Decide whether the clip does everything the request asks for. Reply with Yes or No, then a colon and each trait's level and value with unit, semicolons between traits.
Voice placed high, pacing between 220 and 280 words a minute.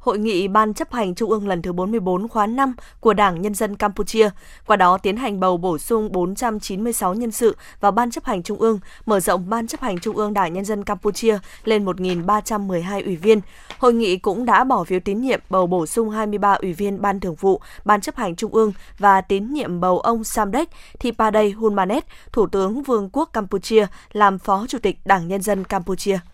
No: high, 210 Hz; average, 205 wpm